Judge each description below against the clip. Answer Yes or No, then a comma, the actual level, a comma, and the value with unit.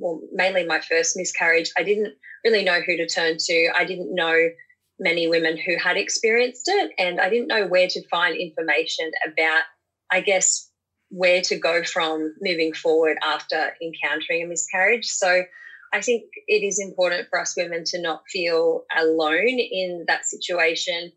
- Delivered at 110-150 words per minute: No, average, 165 wpm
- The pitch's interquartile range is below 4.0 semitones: Yes, average, 3.3 semitones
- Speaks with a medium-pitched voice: Yes, medium, 180 Hz